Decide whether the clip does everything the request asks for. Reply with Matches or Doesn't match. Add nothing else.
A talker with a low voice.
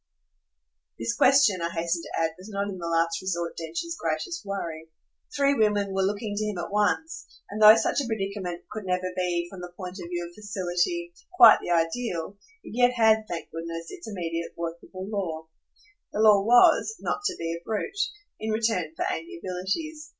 Doesn't match